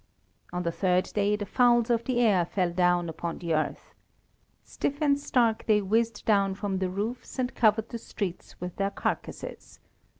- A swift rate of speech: No, average, 175 wpm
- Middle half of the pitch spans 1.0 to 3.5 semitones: No, average, 4.3 semitones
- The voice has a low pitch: No, high, 205 Hz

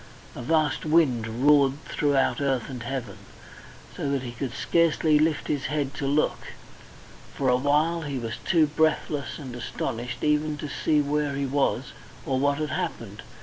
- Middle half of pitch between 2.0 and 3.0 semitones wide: Yes, narrow, 2.5 semitones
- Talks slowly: No, average, 165 wpm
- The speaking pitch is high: No, medium, 140 Hz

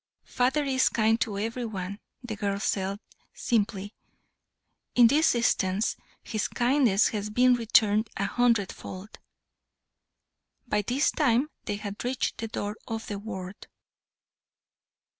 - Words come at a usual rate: No, slow, 125 wpm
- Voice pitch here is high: Yes, high, 220 Hz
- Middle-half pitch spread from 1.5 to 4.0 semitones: Yes, average, 3.2 semitones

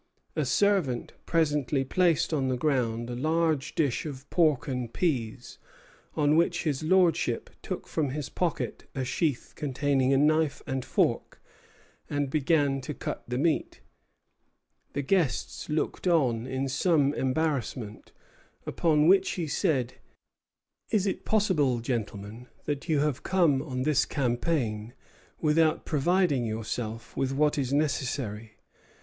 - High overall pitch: No, medium, 140 Hz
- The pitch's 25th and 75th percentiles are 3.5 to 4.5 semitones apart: Yes, average, 3.8 semitones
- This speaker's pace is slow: Yes, slow, 130 wpm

